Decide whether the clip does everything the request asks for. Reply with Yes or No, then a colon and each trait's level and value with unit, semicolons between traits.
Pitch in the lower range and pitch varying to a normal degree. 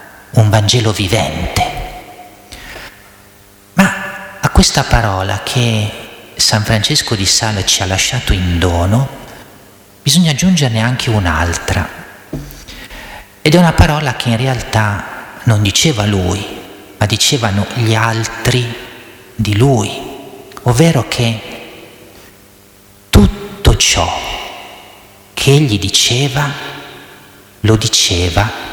Yes: low, 110 Hz; average, 3.8 semitones